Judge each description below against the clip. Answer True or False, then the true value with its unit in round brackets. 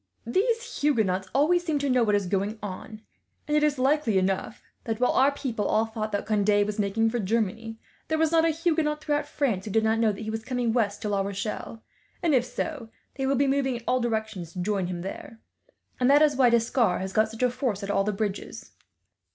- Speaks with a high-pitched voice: True (225 Hz)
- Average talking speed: False (225 wpm)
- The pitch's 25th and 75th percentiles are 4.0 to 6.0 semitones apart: True (5.1 semitones)